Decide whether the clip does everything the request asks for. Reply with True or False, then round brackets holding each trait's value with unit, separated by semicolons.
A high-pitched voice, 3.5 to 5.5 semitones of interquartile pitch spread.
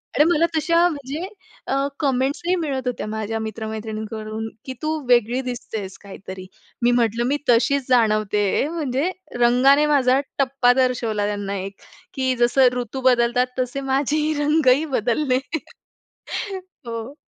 True (250 Hz; 3.9 semitones)